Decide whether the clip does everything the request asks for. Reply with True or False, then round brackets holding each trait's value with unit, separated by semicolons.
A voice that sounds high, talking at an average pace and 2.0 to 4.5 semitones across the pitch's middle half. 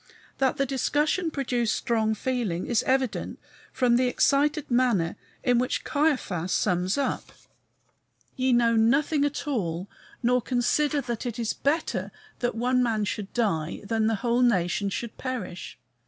True (245 Hz; 150 wpm; 3.5 semitones)